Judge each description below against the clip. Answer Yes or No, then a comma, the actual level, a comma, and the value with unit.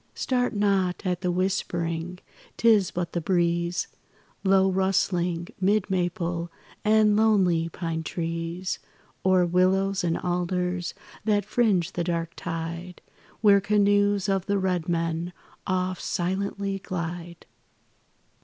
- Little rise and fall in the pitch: Yes, narrow, 2.3 semitones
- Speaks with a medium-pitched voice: Yes, medium, 180 Hz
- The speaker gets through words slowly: Yes, slow, 115 wpm